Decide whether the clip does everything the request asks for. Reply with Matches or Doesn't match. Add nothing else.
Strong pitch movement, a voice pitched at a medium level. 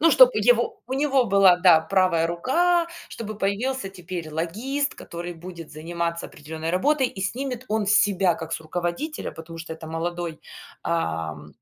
Matches